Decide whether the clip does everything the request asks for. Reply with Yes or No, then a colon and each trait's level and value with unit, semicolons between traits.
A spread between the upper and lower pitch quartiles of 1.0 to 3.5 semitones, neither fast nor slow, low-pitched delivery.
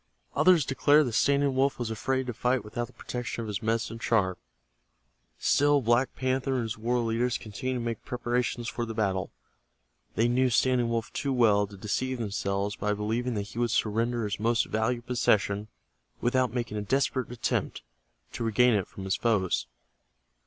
Yes: average, 2.9 semitones; average, 175 wpm; low, 120 Hz